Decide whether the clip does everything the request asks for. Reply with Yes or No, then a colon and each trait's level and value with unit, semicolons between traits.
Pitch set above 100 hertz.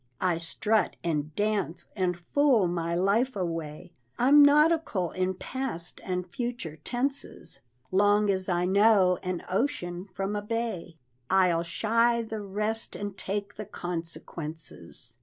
Yes: high, 190 Hz